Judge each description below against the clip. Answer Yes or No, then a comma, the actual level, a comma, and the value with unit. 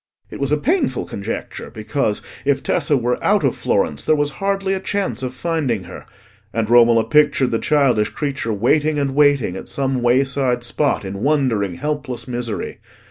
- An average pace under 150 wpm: No, average, 170 wpm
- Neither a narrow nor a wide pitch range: Yes, average, 4.3 semitones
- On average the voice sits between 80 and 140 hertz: Yes, low, 135 Hz